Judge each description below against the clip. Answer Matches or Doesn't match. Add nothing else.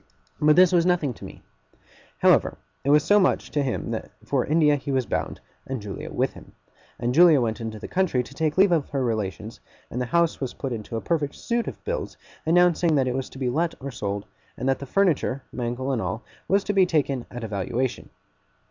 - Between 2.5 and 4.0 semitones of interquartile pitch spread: Doesn't match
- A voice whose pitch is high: Doesn't match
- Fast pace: Matches